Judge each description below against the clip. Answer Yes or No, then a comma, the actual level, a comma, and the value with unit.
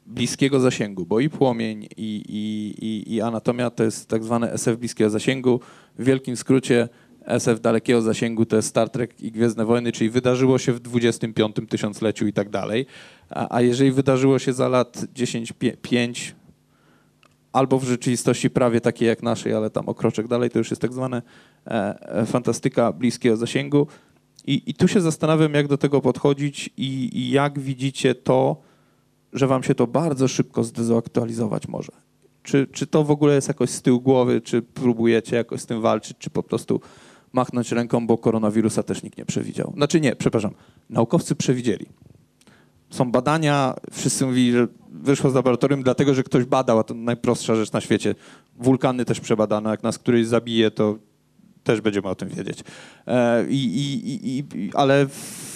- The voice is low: Yes, low, 120 Hz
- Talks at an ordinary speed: No, fast, 170 wpm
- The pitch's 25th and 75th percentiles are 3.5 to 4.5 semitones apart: No, average, 2.8 semitones